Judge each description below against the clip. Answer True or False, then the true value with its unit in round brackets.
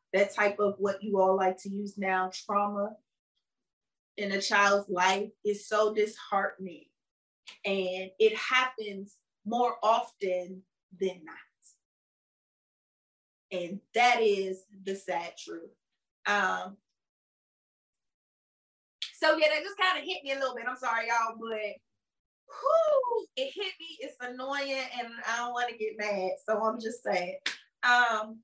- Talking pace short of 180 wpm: True (135 wpm)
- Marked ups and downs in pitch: False (3.9 semitones)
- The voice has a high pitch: True (210 Hz)